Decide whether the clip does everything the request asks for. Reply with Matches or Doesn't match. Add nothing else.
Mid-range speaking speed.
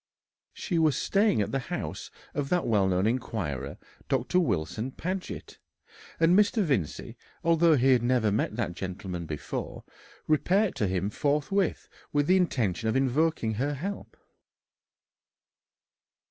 Doesn't match